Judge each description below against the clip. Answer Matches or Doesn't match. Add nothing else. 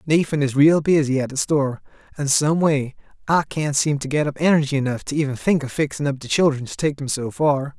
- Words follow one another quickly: Matches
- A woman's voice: Doesn't match